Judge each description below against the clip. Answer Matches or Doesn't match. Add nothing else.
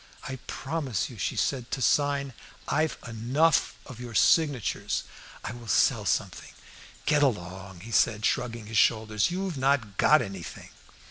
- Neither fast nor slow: Matches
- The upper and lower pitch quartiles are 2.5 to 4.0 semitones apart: Doesn't match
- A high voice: Doesn't match